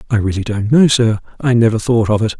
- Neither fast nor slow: No, fast, 250 wpm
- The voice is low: Yes, low, 115 Hz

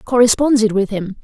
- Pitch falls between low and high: No, high, 225 Hz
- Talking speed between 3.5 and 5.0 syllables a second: No, 5.5 syllables/s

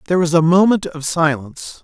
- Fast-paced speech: No, average, 195 wpm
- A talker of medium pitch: Yes, medium, 165 Hz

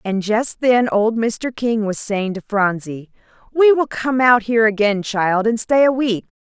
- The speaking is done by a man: No, female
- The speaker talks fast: No, average, 195 wpm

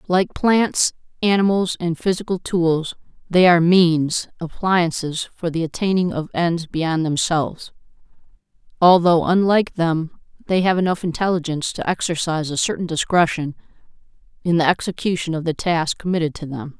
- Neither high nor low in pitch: Yes, medium, 170 Hz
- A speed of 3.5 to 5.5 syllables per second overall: Yes, 5.0 syllables/s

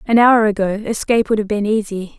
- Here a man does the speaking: No, female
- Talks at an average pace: No, fast, 220 wpm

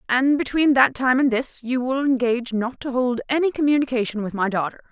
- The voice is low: No, very high, 255 Hz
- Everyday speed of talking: No, fast, 210 wpm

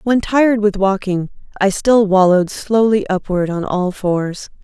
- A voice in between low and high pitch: No, high, 200 Hz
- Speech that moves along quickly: No, average, 155 wpm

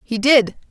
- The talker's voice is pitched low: No, high, 240 Hz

